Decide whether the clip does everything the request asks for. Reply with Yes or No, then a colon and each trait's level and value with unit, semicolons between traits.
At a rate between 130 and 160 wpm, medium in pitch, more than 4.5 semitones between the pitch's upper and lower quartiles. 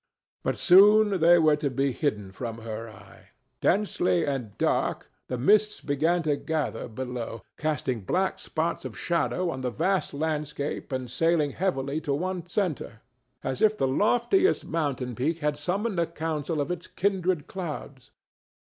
Yes: average, 155 wpm; medium, 155 Hz; average, 5.2 semitones